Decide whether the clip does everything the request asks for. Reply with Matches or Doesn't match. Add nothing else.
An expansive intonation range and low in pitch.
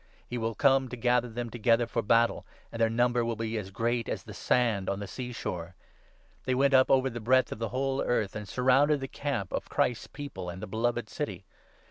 Doesn't match